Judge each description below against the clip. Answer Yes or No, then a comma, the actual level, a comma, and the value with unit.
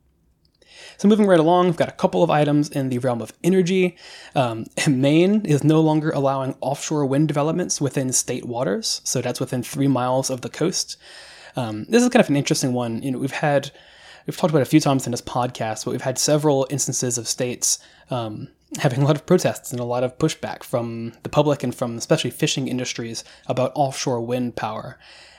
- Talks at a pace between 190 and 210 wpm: Yes, fast, 205 wpm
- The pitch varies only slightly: No, average, 3.9 semitones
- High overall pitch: No, medium, 140 Hz